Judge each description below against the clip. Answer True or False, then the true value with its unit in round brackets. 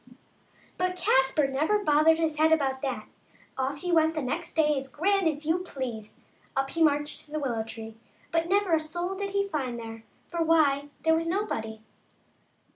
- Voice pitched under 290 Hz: False (310 Hz)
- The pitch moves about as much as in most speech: True (3.8 semitones)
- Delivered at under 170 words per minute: False (185 wpm)